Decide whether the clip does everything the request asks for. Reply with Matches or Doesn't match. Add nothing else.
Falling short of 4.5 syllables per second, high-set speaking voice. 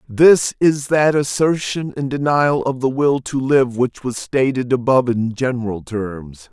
Doesn't match